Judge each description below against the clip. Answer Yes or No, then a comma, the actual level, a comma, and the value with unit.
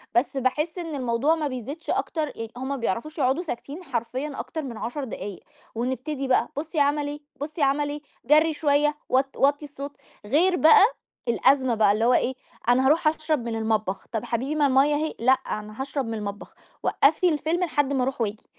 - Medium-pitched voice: No, very high, 275 Hz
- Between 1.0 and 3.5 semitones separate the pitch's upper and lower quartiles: No, average, 4.0 semitones